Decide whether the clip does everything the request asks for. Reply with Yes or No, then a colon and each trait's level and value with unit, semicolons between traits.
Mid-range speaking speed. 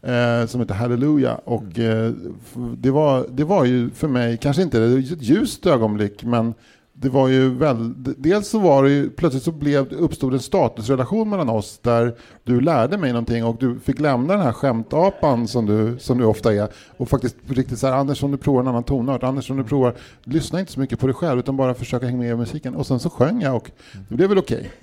No: fast, 235 wpm